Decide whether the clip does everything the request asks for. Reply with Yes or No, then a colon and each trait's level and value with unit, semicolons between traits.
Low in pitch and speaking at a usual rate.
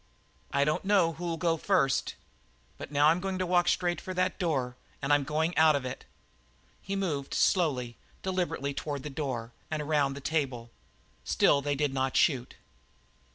No: medium, 150 Hz; average, 165 wpm